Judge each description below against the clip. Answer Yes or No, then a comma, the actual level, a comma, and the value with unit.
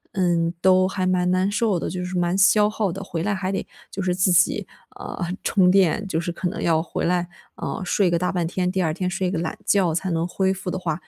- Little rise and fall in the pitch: Yes, narrow, 1.6 semitones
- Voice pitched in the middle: Yes, medium, 180 Hz